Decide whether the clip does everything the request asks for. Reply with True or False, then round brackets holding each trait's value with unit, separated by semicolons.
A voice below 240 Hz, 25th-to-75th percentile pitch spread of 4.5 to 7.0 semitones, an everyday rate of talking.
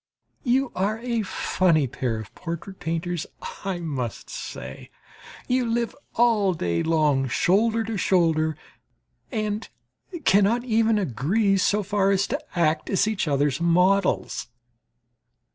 False (190 Hz; 5.6 semitones; 125 wpm)